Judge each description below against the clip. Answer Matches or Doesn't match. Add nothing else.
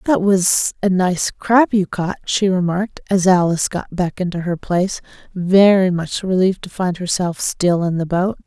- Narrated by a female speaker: Matches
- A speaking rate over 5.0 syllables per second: Doesn't match